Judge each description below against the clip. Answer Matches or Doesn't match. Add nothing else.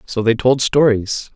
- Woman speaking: Doesn't match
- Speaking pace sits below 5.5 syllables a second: Matches